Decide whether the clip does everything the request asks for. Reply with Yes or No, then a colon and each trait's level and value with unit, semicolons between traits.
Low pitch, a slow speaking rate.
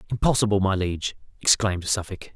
Yes: low, 100 Hz; slow, 125 wpm